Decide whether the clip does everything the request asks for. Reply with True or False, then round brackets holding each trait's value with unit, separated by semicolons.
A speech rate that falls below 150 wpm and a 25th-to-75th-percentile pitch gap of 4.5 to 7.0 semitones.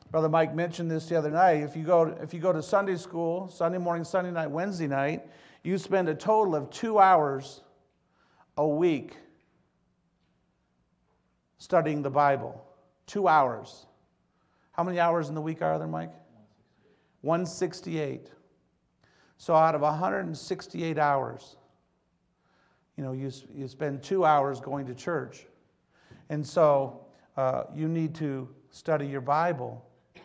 False (140 wpm; 3.7 semitones)